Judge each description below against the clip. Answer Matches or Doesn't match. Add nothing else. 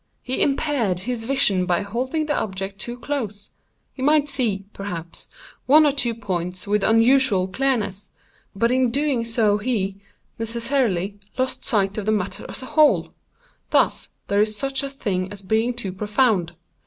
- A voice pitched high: Matches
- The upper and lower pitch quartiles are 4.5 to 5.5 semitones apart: Matches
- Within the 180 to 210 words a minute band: Doesn't match